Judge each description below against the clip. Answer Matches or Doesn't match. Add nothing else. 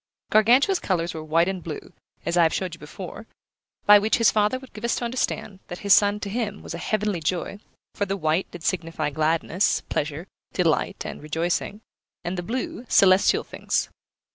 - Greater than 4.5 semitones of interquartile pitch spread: Doesn't match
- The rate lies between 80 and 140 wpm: Doesn't match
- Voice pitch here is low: Doesn't match